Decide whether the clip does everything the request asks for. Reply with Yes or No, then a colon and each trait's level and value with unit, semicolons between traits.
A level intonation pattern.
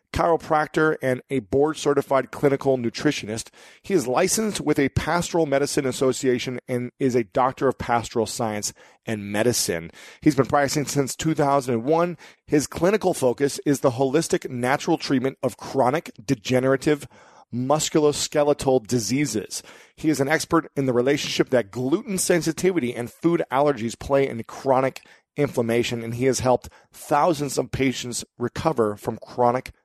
No: average, 3.5 semitones